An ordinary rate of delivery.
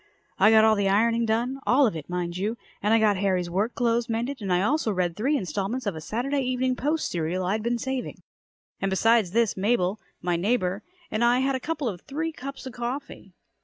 No: fast, 215 wpm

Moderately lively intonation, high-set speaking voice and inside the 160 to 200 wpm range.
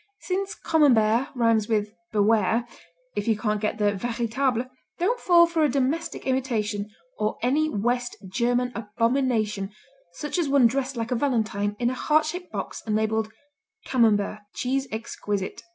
No: average, 4.1 semitones; high, 235 Hz; average, 150 wpm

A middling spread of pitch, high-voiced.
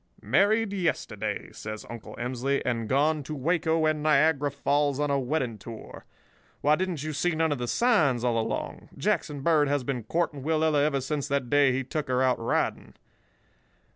No: average, 3.5 semitones; medium, 145 Hz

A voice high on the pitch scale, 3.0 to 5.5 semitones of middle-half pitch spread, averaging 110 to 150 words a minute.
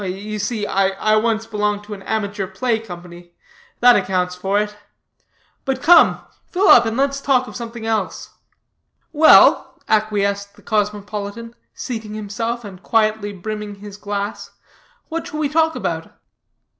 No: high, 210 Hz; narrow, 2.5 semitones; average, 145 wpm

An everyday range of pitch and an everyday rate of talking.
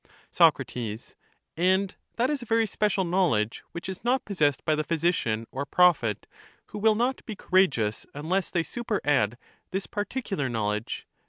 No: wide, 7.0 semitones; average, 150 wpm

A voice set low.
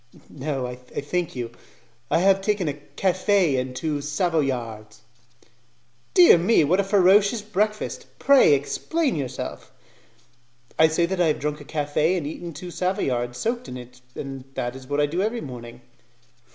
No: medium, 155 Hz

